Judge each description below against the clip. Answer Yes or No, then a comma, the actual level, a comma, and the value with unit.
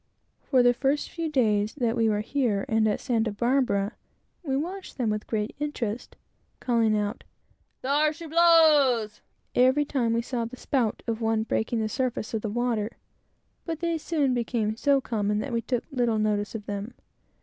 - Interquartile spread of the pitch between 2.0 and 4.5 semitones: Yes, average, 4.1 semitones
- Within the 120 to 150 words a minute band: No, average, 175 wpm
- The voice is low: No, high, 235 Hz